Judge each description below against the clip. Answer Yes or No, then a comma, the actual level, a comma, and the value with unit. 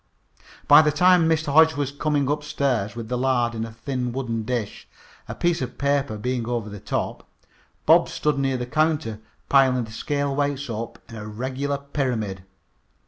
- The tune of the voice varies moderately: Yes, average, 3.7 semitones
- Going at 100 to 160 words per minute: No, average, 175 wpm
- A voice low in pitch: Yes, low, 130 Hz